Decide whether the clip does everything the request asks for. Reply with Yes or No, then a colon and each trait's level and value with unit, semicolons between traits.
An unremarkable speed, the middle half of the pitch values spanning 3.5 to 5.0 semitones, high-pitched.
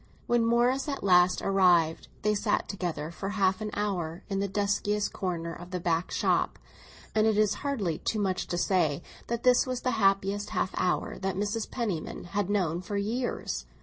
No: average, 180 wpm; average, 3.1 semitones; high, 200 Hz